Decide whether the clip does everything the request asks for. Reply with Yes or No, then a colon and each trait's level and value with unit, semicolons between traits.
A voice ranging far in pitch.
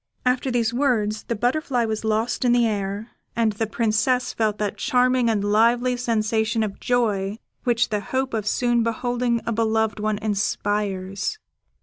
No: narrow, 2.5 semitones